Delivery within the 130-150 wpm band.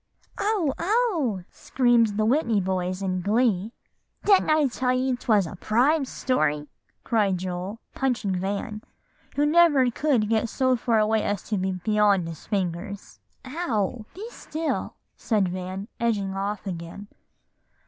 Yes: average, 140 wpm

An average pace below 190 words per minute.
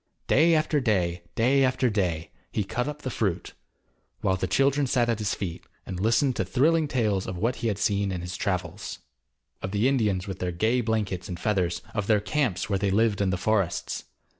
No: fast, 205 wpm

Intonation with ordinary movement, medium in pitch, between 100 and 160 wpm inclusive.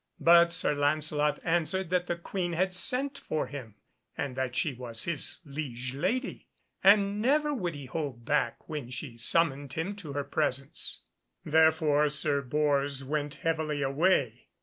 Yes: average, 3.9 semitones; medium, 150 Hz; average, 150 wpm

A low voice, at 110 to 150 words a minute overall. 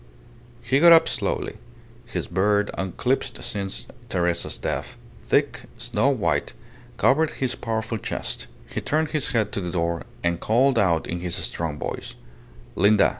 Yes: low, 105 Hz; average, 145 wpm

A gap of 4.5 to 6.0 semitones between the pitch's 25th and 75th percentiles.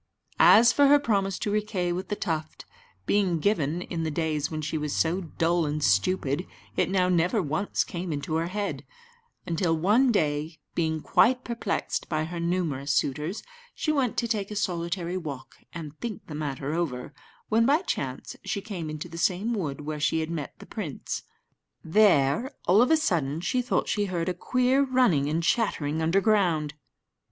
Yes: average, 5.0 semitones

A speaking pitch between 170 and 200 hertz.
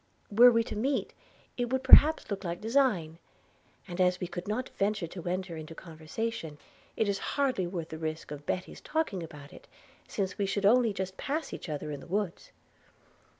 Yes: high, 190 Hz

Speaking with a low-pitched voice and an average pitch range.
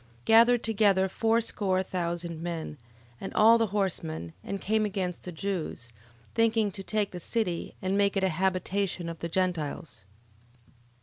No: high, 190 Hz; average, 3.5 semitones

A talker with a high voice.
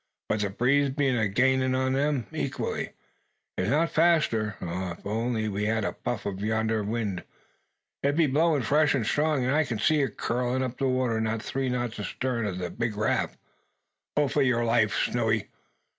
No: low, 120 Hz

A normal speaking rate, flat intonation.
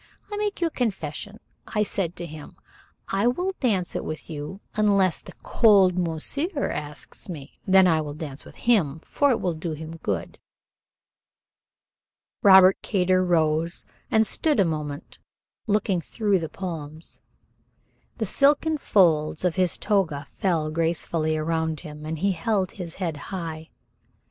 No: average, 150 wpm; average, 4.4 semitones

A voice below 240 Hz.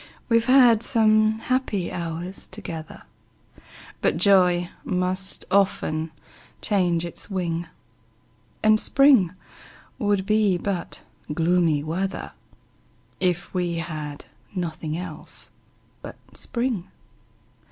Yes: medium, 185 Hz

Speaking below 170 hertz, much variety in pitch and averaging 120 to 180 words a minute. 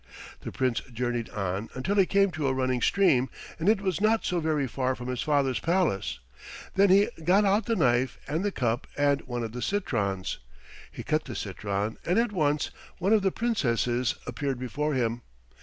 No: medium, 140 Hz; wide, 7.8 semitones; average, 190 wpm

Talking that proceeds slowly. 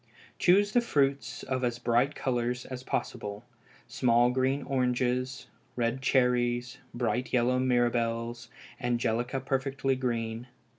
Yes: slow, 110 wpm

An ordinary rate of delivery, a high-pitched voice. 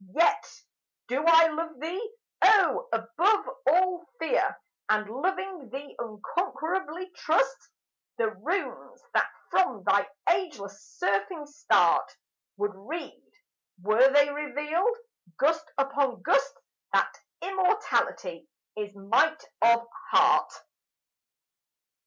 No: slow, 100 wpm; very high, 305 Hz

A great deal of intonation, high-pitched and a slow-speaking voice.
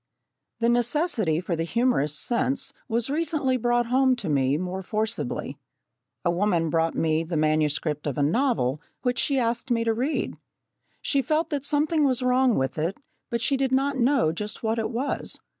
No: wide, 8.1 semitones; high, 235 Hz; average, 175 wpm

